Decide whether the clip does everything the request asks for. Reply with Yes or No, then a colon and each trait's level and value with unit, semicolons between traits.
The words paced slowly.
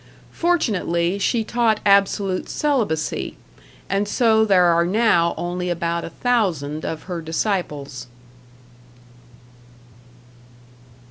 Yes: slow, 90 wpm